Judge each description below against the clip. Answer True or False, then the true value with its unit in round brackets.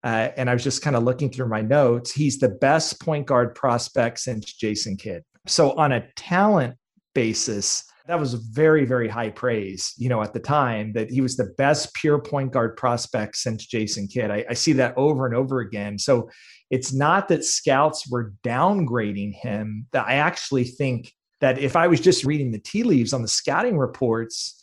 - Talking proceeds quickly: False (195 wpm)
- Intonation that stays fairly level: False (4.3 semitones)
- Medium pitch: False (125 Hz)